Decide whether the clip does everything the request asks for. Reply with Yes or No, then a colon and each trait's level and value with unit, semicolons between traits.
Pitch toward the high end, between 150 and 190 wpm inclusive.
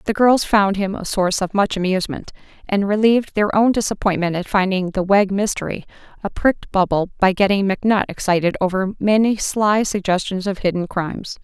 Yes: high, 195 Hz; average, 175 wpm